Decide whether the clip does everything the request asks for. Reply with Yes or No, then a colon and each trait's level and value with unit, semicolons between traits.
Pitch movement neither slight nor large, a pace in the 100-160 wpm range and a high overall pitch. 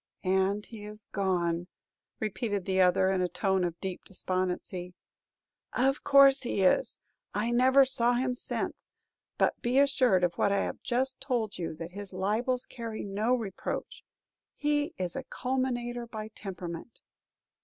Yes: average, 5.0 semitones; average, 150 wpm; high, 210 Hz